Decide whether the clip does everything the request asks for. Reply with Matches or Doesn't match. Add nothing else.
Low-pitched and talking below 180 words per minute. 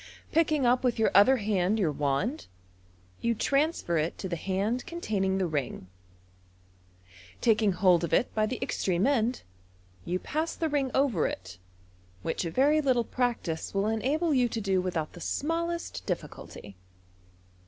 Doesn't match